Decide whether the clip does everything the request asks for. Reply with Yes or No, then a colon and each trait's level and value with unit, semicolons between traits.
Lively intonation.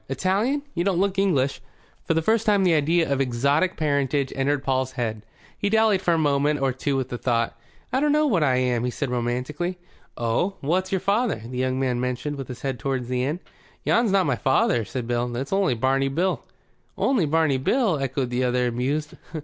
Yes: wide, 6.3 semitones